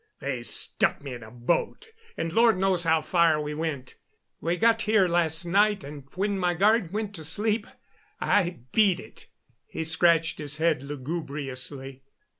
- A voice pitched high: No, medium, 165 Hz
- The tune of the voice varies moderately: Yes, average, 4.8 semitones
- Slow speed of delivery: No, average, 160 wpm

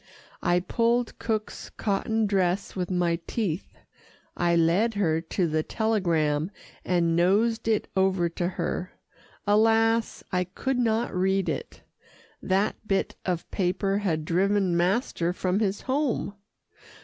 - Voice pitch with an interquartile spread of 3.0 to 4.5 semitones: Yes, average, 3.9 semitones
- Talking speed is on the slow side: Yes, slow, 125 wpm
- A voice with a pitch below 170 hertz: No, high, 190 Hz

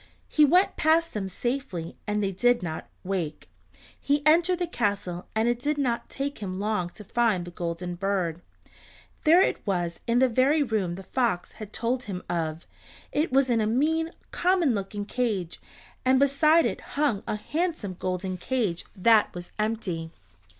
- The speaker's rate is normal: Yes, average, 170 wpm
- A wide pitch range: Yes, wide, 7.1 semitones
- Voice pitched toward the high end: Yes, high, 220 Hz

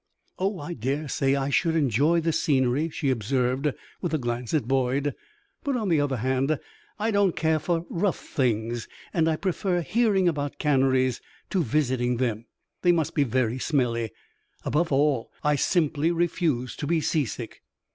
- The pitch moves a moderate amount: Yes, average, 4.4 semitones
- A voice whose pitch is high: No, medium, 145 Hz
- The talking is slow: No, average, 165 wpm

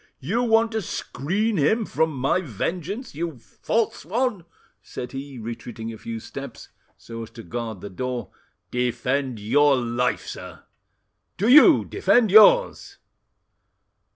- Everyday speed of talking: No, slow, 130 wpm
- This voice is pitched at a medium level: Yes, medium, 145 Hz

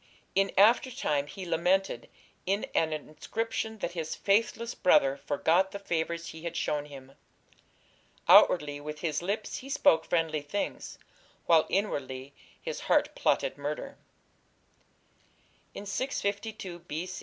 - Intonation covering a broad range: No, average, 4.8 semitones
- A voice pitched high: No, medium, 170 Hz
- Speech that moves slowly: Yes, slow, 125 wpm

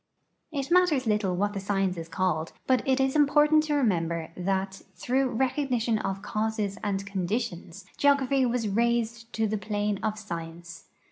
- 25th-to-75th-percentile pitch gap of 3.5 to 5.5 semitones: Yes, average, 5.0 semitones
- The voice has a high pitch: Yes, high, 215 Hz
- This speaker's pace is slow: No, average, 155 wpm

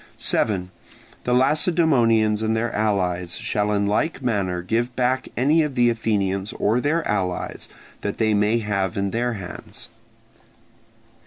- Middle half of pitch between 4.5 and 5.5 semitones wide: No, average, 3.7 semitones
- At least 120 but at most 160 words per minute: Yes, average, 140 wpm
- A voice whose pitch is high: No, low, 110 Hz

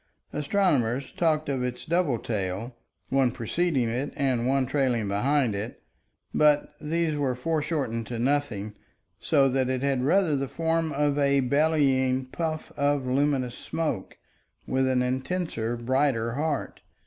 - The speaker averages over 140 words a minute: No, slow, 135 wpm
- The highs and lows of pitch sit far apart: No, average, 3.2 semitones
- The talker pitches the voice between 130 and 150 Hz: Yes, low, 135 Hz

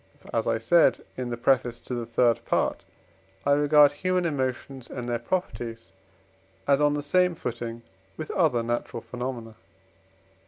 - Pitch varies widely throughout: No, average, 3.8 semitones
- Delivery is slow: No, average, 155 wpm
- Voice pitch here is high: No, low, 125 Hz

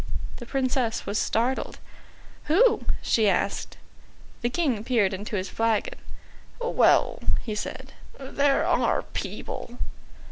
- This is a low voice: No, high, 240 Hz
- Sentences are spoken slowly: Yes, slow, 110 wpm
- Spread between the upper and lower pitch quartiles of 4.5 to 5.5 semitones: No, average, 4.0 semitones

